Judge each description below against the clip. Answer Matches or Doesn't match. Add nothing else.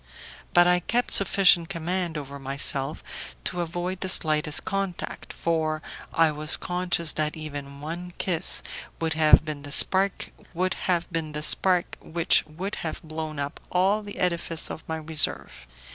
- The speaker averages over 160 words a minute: Doesn't match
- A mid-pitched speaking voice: Matches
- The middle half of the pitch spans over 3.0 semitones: Doesn't match